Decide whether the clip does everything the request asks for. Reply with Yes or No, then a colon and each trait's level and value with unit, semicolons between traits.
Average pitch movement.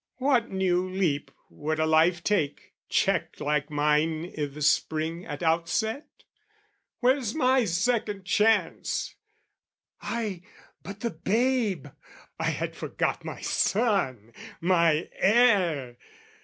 No: wide, 6.0 semitones